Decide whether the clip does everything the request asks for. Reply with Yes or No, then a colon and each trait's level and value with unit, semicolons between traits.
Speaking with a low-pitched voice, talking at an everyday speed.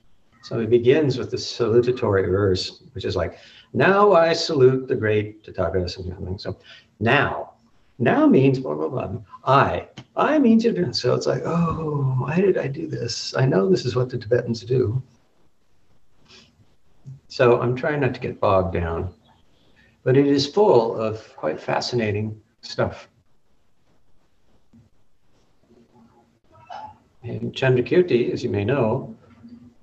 No: low, 120 Hz; slow, 130 wpm